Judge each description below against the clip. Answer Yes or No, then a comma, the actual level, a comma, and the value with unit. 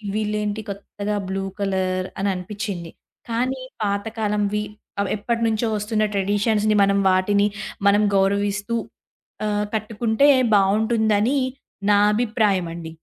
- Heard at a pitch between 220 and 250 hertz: No, high, 205 Hz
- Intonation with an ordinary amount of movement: No, narrow, 1.7 semitones